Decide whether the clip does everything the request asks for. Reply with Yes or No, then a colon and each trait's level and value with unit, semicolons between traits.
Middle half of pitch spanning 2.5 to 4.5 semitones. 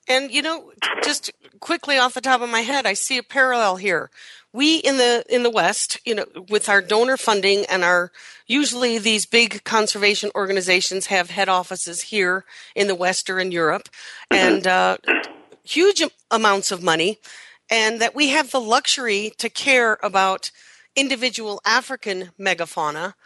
No: average, 4.9 semitones